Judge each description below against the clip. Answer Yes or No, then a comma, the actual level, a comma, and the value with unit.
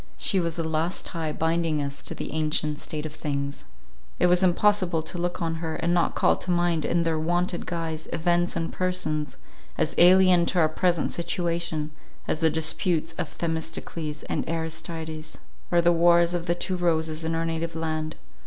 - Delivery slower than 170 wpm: No, average, 180 wpm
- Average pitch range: No, narrow, 1.7 semitones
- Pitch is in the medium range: Yes, medium, 165 Hz